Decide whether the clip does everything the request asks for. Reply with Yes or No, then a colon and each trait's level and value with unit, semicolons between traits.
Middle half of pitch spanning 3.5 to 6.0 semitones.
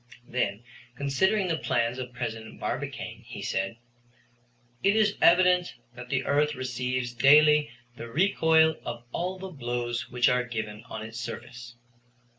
Yes: average, 5.0 semitones